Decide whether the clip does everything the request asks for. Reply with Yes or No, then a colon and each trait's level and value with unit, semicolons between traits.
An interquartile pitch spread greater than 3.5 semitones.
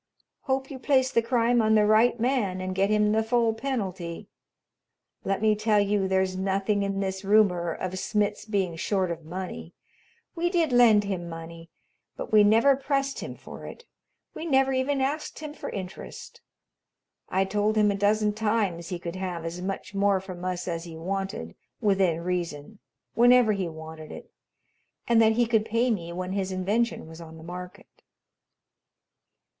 Yes: average, 3.9 semitones